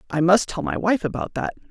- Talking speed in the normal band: No, fast, 245 wpm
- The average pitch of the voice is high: Yes, high, 195 Hz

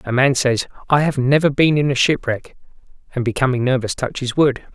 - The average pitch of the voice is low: Yes, low, 130 Hz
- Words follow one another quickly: No, average, 190 wpm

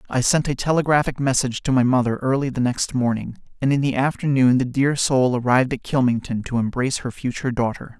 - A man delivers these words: Yes, male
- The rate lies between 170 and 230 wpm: Yes, fast, 205 wpm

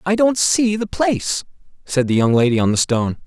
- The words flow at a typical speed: No, fast, 220 wpm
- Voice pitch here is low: No, medium, 160 Hz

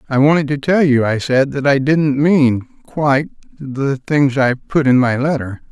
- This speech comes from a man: Yes, male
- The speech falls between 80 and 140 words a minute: No, average, 200 wpm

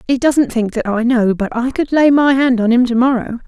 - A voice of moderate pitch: No, high, 245 Hz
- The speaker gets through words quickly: Yes, fast, 275 wpm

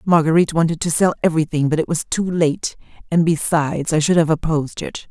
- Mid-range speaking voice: Yes, medium, 160 Hz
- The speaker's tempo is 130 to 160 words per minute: No, average, 200 wpm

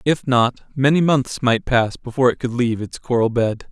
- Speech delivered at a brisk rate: Yes, fast, 210 wpm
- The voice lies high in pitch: No, low, 125 Hz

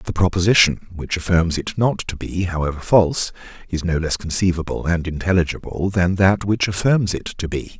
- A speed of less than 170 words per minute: No, average, 175 wpm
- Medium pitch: No, very low, 90 Hz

